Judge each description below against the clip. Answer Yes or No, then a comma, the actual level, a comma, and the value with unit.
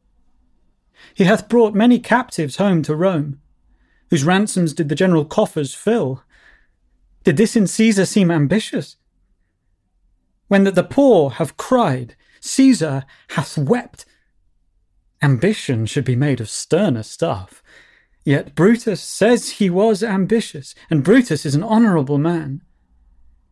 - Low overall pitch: No, medium, 160 Hz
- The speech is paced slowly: Yes, slow, 125 wpm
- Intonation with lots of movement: Yes, wide, 8.9 semitones